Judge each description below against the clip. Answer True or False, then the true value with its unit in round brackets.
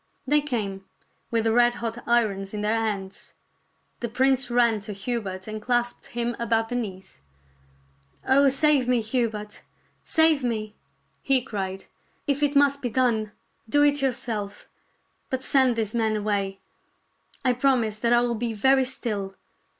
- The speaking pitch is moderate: False (235 Hz)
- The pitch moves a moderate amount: True (3.5 semitones)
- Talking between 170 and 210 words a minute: False (160 wpm)